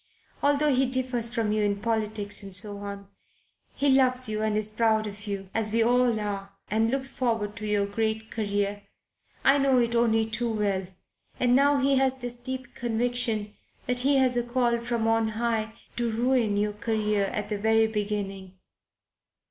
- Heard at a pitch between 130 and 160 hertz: No, high, 225 Hz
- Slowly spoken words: No, average, 180 wpm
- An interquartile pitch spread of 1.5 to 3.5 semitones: Yes, average, 2.8 semitones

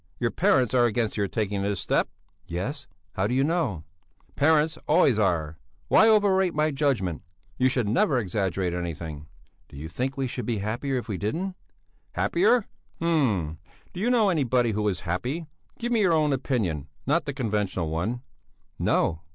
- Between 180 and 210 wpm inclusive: No, average, 170 wpm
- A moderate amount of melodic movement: No, wide, 8.2 semitones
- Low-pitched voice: Yes, low, 120 Hz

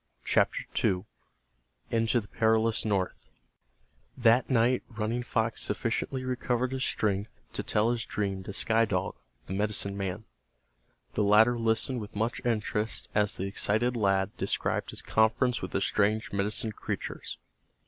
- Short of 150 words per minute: Yes, average, 140 wpm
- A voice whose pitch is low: Yes, low, 110 Hz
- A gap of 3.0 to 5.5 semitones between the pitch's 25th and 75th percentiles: No, narrow, 2.4 semitones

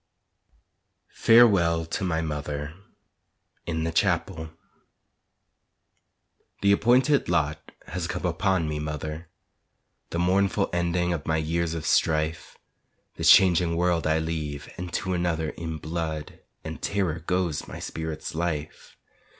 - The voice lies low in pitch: Yes, very low, 85 Hz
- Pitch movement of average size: No, narrow, 2.2 semitones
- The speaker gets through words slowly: Yes, slow, 120 wpm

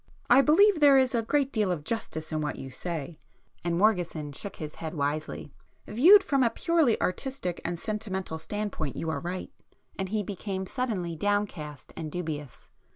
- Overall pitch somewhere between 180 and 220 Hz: Yes, medium, 185 Hz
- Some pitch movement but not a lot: No, wide, 6.5 semitones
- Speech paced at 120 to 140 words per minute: No, average, 165 wpm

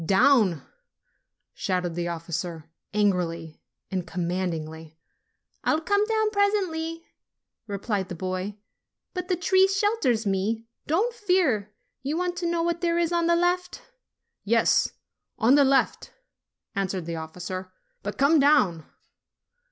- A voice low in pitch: No, high, 225 Hz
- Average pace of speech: No, slow, 130 wpm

